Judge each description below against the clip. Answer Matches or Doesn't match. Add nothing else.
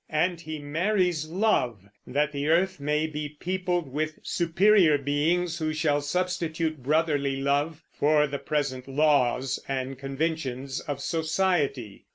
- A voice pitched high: Doesn't match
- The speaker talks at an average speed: Doesn't match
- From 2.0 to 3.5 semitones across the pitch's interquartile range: Matches